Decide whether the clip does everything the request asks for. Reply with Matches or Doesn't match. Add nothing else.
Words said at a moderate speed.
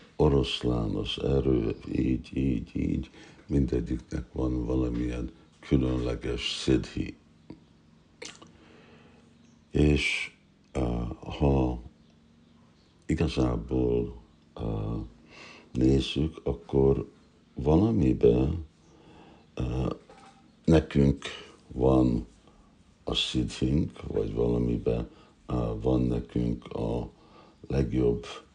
Doesn't match